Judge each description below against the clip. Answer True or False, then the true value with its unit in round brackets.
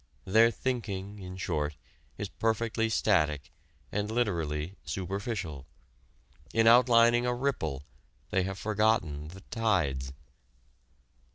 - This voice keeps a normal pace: False (100 wpm)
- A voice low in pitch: True (100 Hz)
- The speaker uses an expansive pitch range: True (5.9 semitones)